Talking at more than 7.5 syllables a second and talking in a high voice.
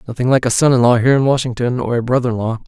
No: 7.7 syllables/s; low, 125 Hz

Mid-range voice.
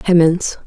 Yes: medium, 175 Hz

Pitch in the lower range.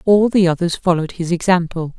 No: medium, 175 Hz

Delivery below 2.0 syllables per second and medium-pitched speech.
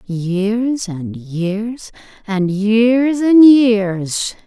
No: 1.8 syllables/s; high, 210 Hz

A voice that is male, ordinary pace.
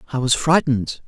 Yes: male; average, 165 wpm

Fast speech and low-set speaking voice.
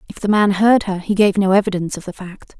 No: fast, 275 wpm; high, 195 Hz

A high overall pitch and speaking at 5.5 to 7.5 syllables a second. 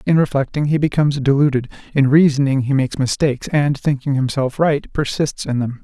No: medium, 140 Hz; 5.7 syllables/s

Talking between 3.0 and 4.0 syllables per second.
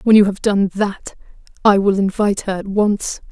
No: 5.0 syllables/s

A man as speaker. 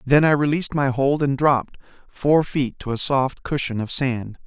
Yes: male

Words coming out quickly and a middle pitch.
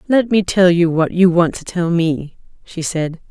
Yes: fast, 220 wpm; medium, 175 Hz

